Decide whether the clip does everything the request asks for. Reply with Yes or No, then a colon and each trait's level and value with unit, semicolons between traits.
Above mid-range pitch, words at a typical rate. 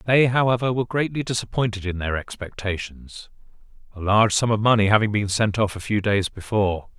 No: low, 105 Hz; average, 180 wpm